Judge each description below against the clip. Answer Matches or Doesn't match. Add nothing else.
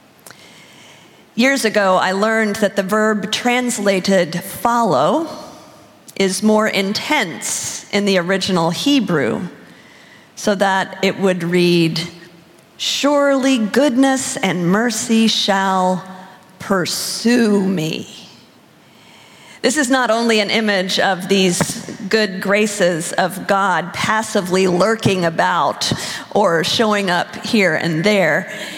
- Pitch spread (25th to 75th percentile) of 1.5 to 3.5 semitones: Matches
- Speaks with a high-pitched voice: Matches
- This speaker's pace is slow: Matches